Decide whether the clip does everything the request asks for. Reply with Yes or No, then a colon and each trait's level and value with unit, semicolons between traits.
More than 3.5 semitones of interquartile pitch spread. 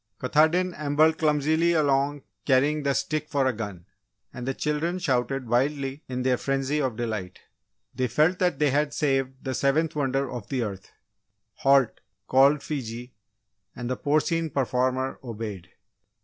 No: average, 3.0 semitones